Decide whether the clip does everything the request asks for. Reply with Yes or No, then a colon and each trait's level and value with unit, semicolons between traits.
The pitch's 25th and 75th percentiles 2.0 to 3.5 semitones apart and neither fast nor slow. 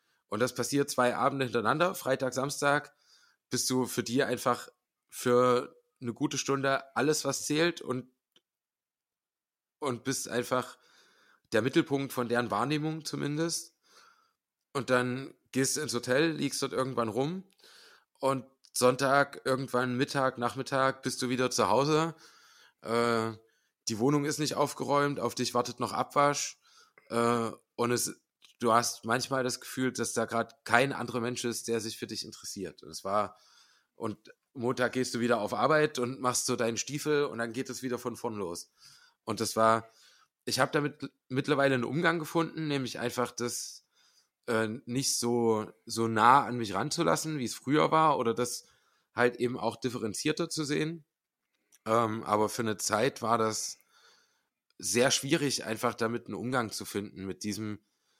Yes: average, 3.2 semitones; average, 160 wpm